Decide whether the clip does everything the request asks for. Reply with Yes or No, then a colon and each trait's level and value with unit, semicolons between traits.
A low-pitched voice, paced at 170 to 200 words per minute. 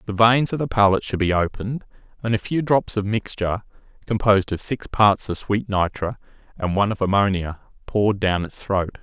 Yes: low, 105 Hz; average, 195 wpm